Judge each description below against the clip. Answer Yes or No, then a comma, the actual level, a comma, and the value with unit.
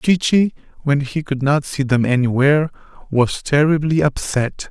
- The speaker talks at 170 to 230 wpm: No, average, 155 wpm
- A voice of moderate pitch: Yes, medium, 145 Hz